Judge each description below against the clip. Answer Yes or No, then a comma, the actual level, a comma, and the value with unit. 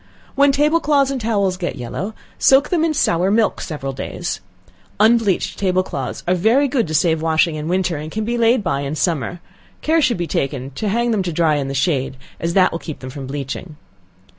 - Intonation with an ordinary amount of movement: No, wide, 7.1 semitones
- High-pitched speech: No, medium, 180 Hz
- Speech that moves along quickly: Yes, fast, 215 wpm